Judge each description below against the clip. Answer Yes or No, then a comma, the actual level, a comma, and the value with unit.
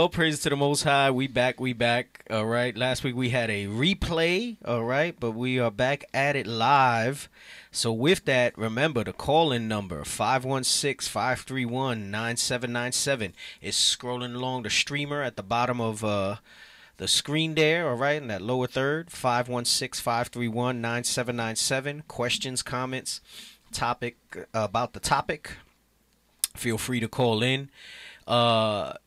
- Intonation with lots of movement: No, average, 3.1 semitones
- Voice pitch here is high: No, low, 125 Hz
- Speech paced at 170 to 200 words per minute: No, average, 150 wpm